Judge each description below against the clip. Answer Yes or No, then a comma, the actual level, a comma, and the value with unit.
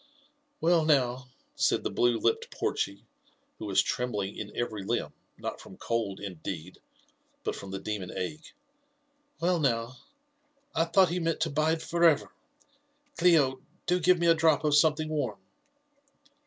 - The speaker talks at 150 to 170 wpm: Yes, average, 165 wpm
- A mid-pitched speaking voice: Yes, medium, 150 Hz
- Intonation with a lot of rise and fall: Yes, wide, 6.7 semitones